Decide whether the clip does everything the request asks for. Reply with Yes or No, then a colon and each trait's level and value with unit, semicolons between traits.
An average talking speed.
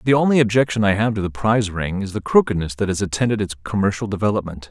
No: fast, 230 wpm